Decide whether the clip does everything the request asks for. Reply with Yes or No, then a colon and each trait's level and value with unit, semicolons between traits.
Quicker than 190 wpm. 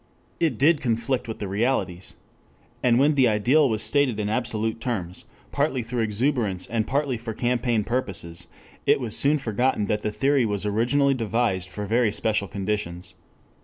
No: average, 165 wpm